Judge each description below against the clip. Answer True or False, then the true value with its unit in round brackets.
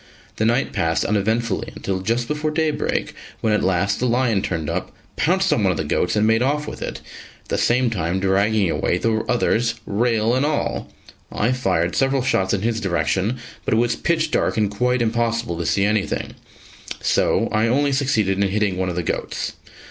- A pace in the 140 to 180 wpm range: False (195 wpm)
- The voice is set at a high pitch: False (110 Hz)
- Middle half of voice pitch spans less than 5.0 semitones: True (4.4 semitones)